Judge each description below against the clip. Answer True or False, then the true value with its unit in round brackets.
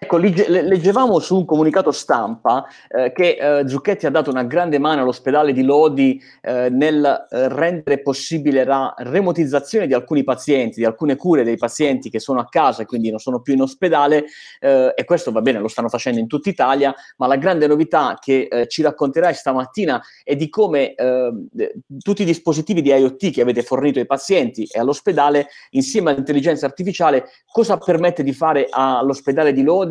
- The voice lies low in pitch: False (145 Hz)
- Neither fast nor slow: False (180 wpm)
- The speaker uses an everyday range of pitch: True (3.7 semitones)